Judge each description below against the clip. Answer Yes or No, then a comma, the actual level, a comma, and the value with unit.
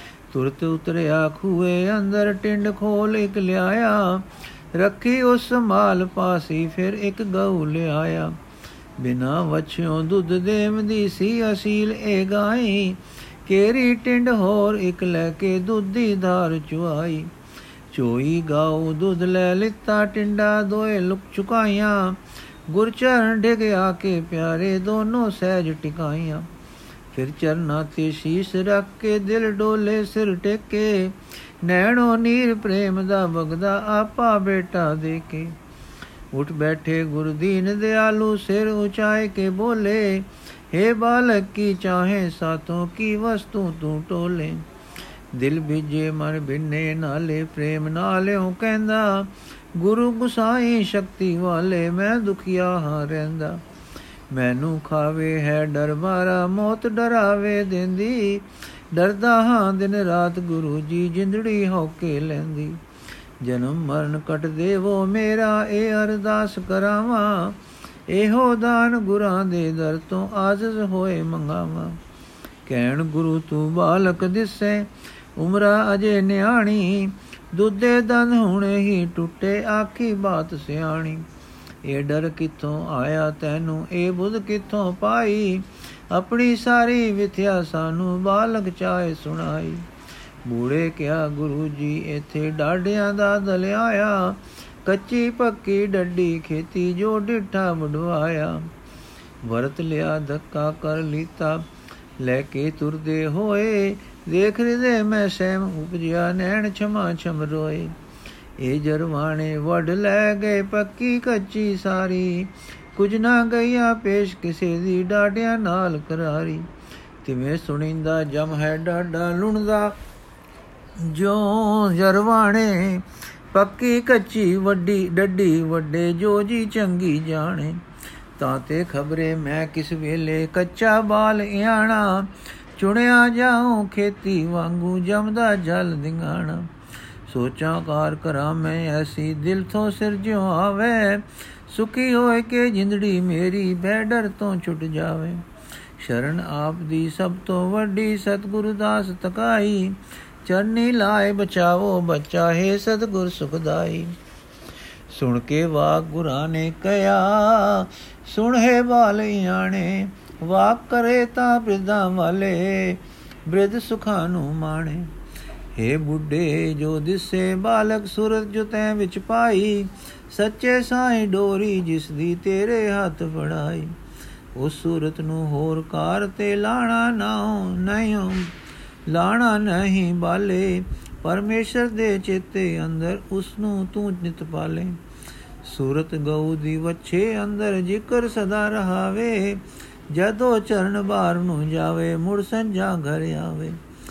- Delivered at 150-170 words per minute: No, average, 115 wpm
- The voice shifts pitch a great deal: No, average, 4.6 semitones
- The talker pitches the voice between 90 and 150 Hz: No, medium, 185 Hz